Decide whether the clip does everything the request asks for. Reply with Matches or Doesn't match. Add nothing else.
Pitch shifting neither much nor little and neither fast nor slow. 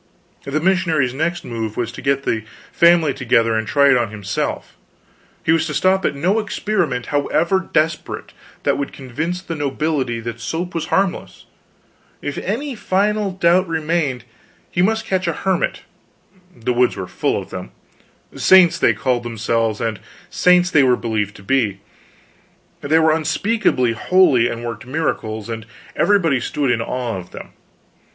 Doesn't match